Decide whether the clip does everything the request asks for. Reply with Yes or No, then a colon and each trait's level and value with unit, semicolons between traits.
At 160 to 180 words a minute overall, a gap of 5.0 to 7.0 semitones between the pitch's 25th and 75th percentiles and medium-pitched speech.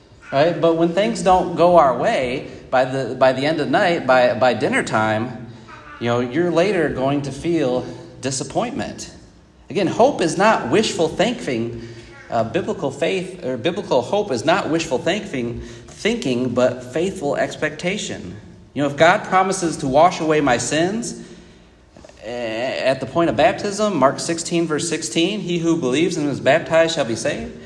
Yes: average, 165 wpm; average, 5.3 semitones; medium, 150 Hz